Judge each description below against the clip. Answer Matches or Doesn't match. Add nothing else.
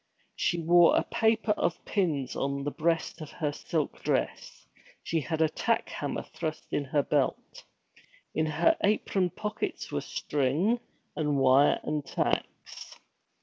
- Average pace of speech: Matches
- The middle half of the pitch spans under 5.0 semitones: Matches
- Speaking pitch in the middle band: Matches